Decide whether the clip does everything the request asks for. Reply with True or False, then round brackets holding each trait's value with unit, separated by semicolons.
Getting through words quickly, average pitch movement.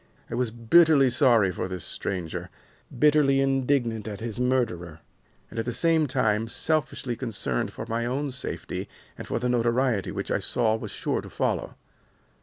False (165 wpm; 3.6 semitones)